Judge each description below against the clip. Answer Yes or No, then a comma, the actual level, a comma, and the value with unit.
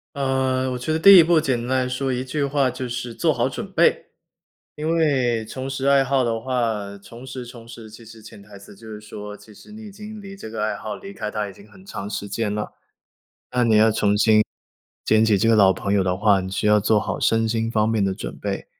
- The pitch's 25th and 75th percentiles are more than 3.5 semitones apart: Yes, average, 3.9 semitones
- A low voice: Yes, low, 115 Hz